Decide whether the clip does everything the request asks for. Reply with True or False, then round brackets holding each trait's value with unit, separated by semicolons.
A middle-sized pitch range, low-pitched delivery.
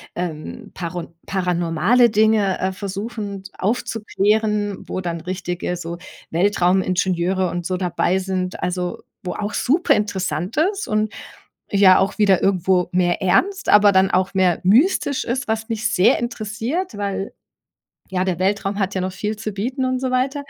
False (3.0 semitones; 195 Hz)